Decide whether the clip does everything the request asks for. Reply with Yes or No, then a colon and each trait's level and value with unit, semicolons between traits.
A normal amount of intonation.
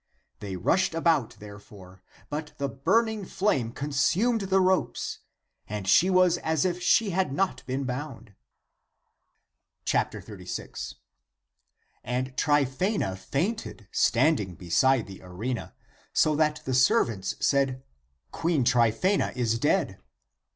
No: wide, 7.6 semitones